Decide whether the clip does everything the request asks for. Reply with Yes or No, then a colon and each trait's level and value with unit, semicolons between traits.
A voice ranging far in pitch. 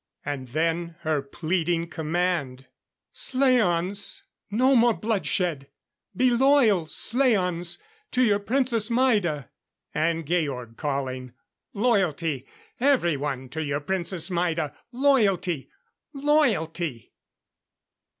Yes: wide, 7.2 semitones